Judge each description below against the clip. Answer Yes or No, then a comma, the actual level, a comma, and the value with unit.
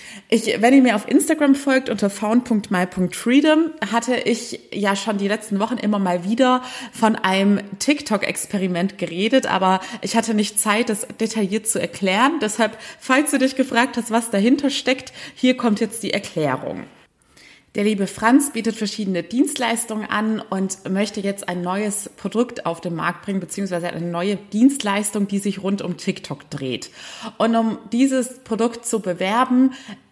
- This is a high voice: Yes, high, 220 Hz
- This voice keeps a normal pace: Yes, average, 155 wpm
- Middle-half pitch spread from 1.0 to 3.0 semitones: No, average, 3.6 semitones